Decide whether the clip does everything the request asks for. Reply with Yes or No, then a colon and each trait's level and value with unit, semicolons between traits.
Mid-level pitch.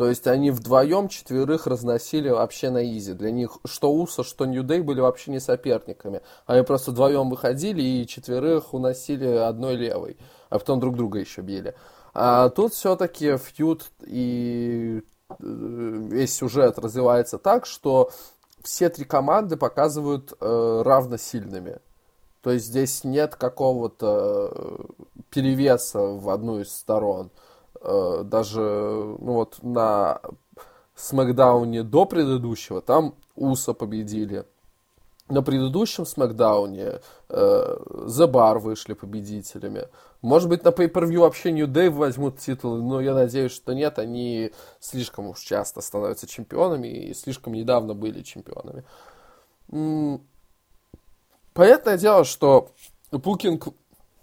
No: low, 130 Hz